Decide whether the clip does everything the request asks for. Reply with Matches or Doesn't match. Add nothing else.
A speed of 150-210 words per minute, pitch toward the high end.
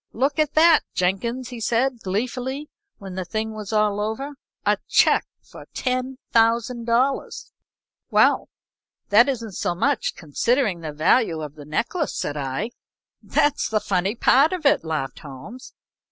Doesn't match